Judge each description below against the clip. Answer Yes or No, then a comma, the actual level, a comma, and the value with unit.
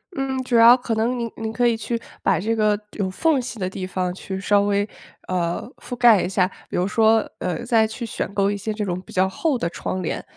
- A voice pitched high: Yes, high, 215 Hz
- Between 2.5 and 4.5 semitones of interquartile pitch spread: Yes, average, 3.7 semitones